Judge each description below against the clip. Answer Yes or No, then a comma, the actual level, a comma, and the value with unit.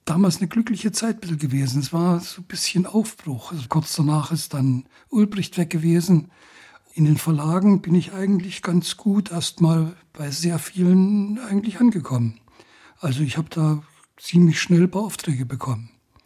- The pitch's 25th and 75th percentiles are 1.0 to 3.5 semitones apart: No, average, 3.9 semitones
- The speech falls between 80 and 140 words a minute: No, average, 150 wpm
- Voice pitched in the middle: Yes, medium, 170 Hz